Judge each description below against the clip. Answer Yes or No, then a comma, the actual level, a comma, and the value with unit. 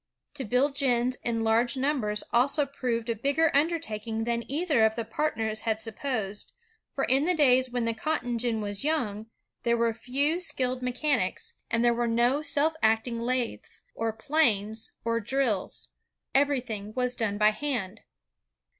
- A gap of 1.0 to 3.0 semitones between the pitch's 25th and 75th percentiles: No, average, 3.8 semitones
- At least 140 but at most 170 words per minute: Yes, average, 165 wpm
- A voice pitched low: No, high, 240 Hz